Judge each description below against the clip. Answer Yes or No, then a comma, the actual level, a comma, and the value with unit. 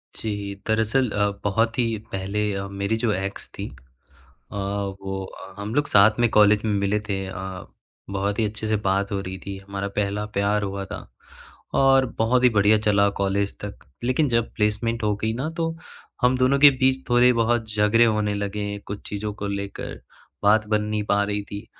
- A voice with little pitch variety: Yes, narrow, 2.2 semitones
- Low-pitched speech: Yes, low, 105 Hz